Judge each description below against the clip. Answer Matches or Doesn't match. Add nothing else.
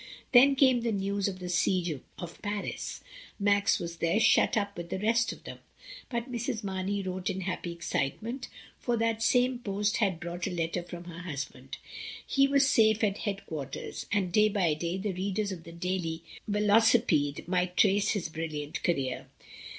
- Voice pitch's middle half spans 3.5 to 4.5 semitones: Matches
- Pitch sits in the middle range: Doesn't match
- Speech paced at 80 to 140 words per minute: Doesn't match